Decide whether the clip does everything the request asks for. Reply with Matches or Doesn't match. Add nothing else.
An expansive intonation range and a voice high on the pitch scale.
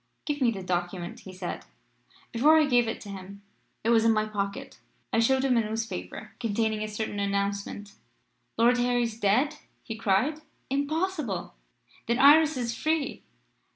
Doesn't match